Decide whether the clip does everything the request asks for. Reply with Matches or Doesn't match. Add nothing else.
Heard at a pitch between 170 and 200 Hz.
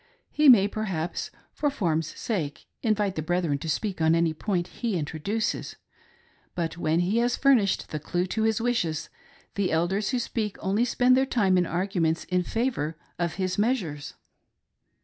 Matches